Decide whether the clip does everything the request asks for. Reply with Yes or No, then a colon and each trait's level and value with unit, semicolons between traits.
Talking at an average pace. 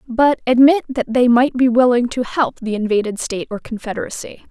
Yes: average, 185 wpm